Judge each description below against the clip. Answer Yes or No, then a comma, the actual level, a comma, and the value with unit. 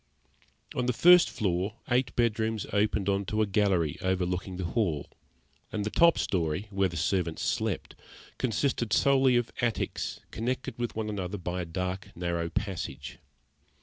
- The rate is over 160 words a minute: No, average, 150 wpm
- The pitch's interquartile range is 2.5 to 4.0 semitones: No, average, 4.5 semitones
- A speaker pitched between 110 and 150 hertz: No, low, 100 Hz